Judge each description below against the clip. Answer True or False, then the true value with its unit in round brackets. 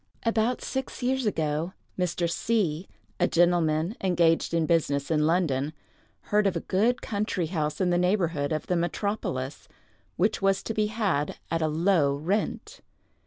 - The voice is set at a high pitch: False (175 Hz)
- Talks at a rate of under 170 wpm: True (155 wpm)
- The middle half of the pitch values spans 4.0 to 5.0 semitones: True (4.5 semitones)